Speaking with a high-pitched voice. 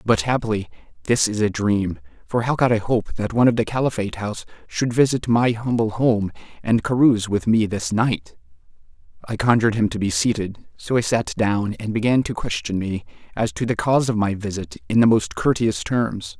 No: low, 110 Hz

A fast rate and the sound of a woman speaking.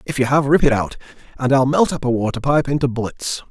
No: fast, 255 wpm; male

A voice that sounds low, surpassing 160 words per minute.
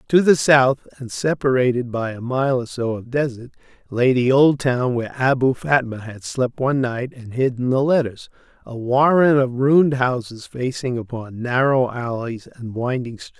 Yes: low, 125 Hz; average, 175 wpm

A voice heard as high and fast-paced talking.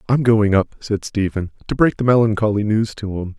No: low, 105 Hz; fast, 215 wpm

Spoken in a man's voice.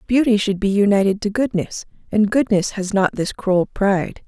No: female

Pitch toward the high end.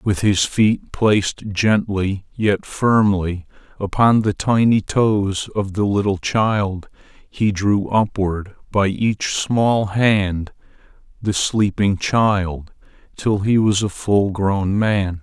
No: low, 100 Hz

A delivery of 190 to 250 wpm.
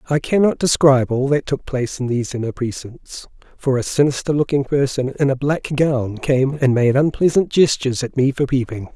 Yes: average, 195 wpm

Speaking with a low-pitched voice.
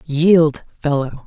No: medium, 155 Hz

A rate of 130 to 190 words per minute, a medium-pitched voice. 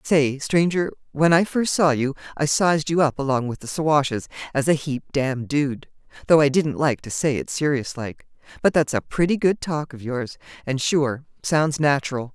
No: average, 200 wpm; medium, 145 Hz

